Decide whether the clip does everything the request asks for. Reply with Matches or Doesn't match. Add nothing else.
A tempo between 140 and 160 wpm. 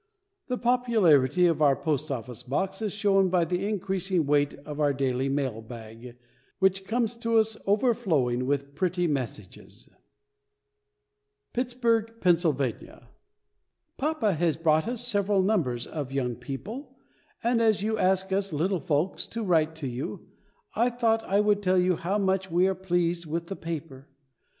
Matches